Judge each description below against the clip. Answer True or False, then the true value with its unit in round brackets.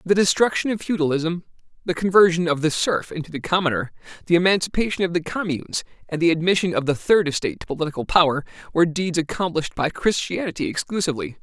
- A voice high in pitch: False (170 Hz)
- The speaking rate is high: False (175 wpm)